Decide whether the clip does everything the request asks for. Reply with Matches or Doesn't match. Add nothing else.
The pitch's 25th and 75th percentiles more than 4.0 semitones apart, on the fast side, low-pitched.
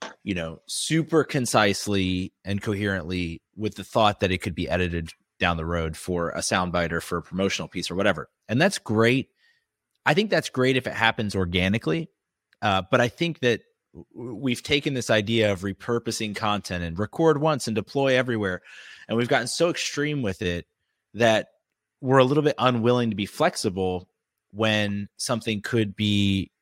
Doesn't match